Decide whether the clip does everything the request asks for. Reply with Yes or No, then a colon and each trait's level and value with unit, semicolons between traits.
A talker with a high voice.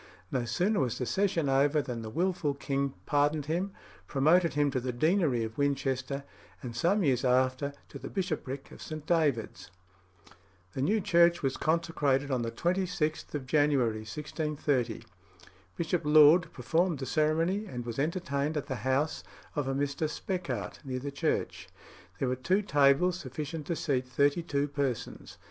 No: medium, 145 Hz